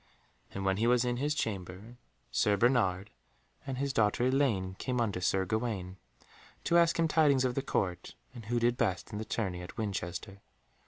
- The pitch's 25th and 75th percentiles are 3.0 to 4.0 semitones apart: No, average, 4.9 semitones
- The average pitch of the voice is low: Yes, low, 110 Hz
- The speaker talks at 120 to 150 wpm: No, average, 180 wpm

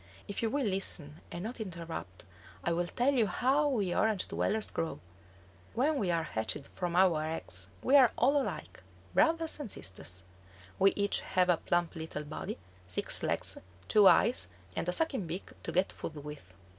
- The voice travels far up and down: Yes, wide, 6.6 semitones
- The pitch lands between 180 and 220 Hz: Yes, medium, 185 Hz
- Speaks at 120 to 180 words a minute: Yes, average, 175 wpm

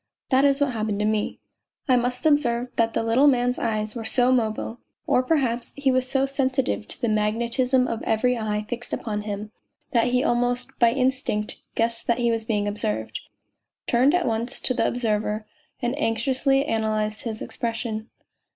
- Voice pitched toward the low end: No, high, 235 Hz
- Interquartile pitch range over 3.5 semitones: No, average, 2.8 semitones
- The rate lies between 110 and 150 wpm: No, average, 180 wpm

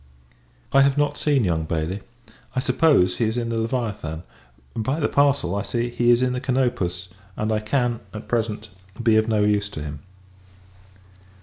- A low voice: Yes, low, 115 Hz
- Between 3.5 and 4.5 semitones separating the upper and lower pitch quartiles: Yes, average, 3.9 semitones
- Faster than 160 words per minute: Yes, average, 180 wpm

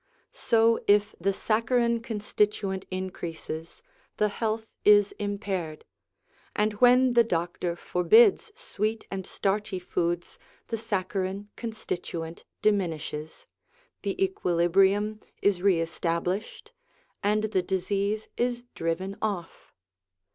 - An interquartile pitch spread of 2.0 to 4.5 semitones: Yes, average, 3.5 semitones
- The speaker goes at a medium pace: No, slow, 100 wpm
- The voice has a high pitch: Yes, high, 200 Hz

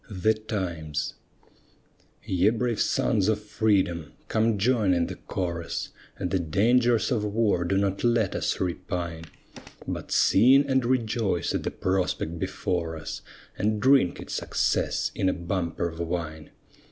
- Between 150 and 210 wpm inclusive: No, average, 140 wpm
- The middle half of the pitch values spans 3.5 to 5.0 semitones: Yes, average, 4.3 semitones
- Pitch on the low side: Yes, very low, 95 Hz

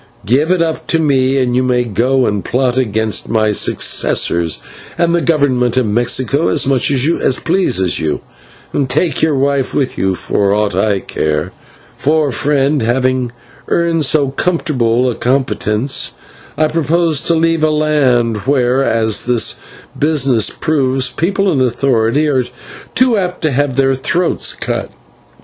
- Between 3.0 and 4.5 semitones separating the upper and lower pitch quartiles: Yes, average, 4.2 semitones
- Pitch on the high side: No, low, 135 Hz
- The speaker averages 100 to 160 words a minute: Yes, average, 150 wpm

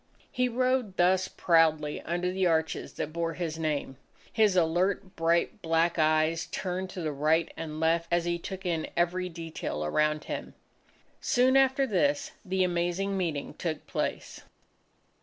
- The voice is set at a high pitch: No, medium, 170 Hz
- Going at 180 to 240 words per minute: No, average, 150 wpm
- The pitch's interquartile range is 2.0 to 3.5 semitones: Yes, average, 2.7 semitones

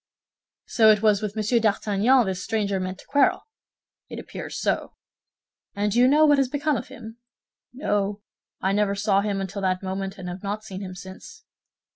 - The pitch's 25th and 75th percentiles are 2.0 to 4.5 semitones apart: Yes, narrow, 2.5 semitones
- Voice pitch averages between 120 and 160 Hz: No, high, 205 Hz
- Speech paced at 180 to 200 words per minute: Yes, average, 185 wpm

